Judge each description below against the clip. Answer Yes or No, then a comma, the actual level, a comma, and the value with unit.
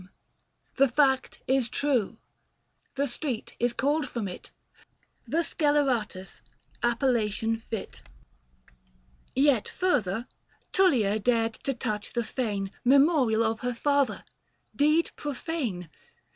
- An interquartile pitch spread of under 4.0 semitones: No, average, 4.4 semitones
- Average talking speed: No, slow, 115 wpm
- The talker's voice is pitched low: No, high, 245 Hz